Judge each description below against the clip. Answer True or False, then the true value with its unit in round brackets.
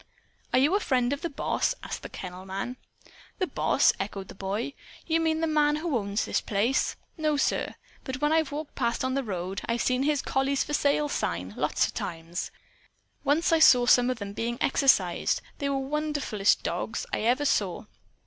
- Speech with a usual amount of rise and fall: False (6.2 semitones)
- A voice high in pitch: True (265 Hz)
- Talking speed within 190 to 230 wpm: True (195 wpm)